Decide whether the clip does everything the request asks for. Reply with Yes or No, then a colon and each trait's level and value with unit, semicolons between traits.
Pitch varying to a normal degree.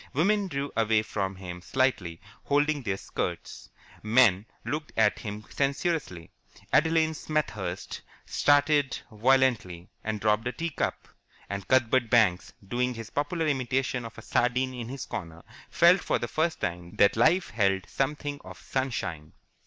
No: wide, 6.0 semitones